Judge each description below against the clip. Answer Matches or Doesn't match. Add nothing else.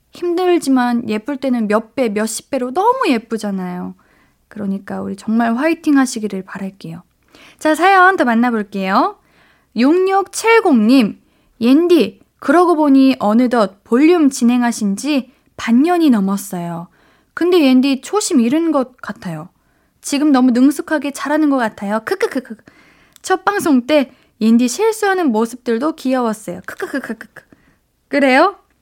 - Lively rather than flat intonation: Matches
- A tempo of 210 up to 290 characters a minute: Matches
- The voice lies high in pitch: Matches